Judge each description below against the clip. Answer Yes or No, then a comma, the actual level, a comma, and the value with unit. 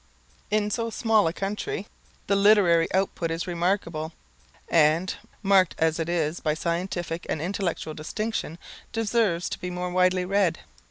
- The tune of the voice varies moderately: Yes, average, 3.3 semitones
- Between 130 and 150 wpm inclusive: Yes, average, 145 wpm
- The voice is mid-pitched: Yes, medium, 180 Hz